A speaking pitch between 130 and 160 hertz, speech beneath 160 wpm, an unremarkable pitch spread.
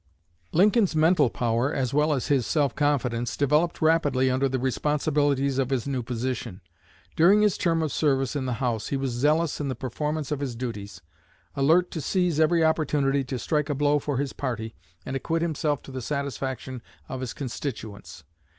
No: medium, 140 Hz; average, 180 wpm; average, 3.1 semitones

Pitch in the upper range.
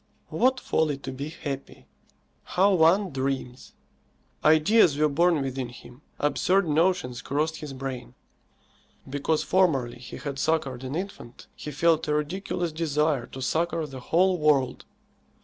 No: medium, 150 Hz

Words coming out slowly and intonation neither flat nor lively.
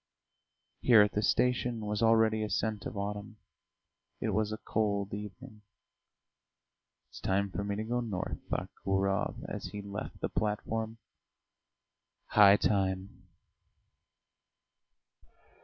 No: slow, 120 wpm; narrow, 1.7 semitones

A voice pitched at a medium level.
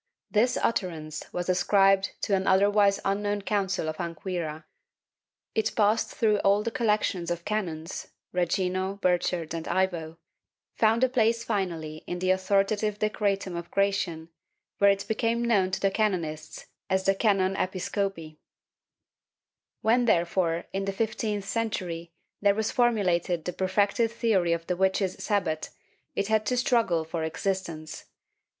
No: high, 195 Hz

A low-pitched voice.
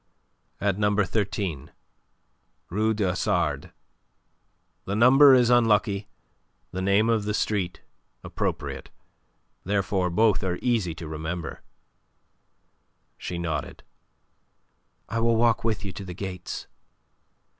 Yes: low, 100 Hz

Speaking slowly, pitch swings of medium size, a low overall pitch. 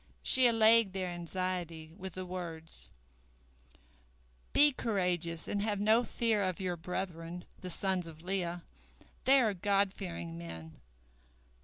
No: slow, 130 wpm; average, 3.5 semitones; medium, 185 Hz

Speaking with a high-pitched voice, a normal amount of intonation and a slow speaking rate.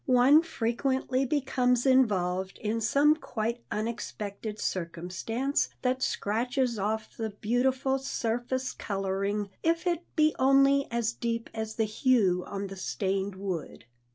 Yes: high, 230 Hz; average, 4.6 semitones; slow, 125 wpm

